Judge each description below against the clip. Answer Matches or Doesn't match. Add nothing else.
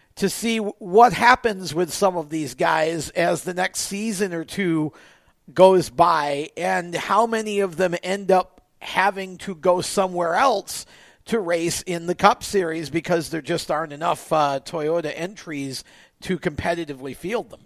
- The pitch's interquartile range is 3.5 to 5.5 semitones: Doesn't match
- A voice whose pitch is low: Doesn't match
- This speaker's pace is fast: Doesn't match